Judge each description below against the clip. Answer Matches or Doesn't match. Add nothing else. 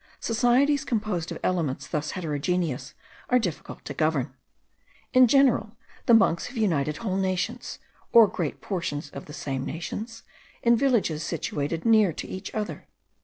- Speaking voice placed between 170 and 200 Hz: Matches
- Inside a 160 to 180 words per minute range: Doesn't match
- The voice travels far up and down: Matches